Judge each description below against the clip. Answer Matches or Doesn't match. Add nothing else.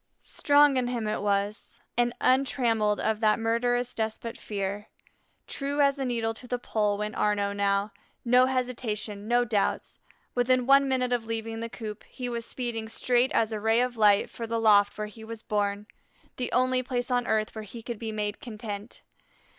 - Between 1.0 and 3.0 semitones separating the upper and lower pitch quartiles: Matches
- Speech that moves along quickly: Doesn't match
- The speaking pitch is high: Matches